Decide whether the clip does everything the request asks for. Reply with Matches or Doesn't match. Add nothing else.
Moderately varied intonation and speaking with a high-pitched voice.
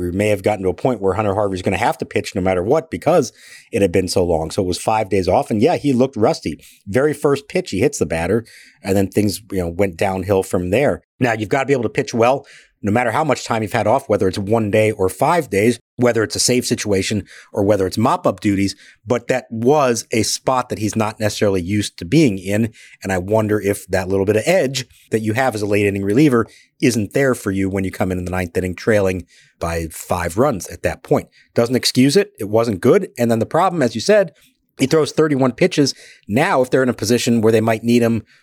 Doesn't match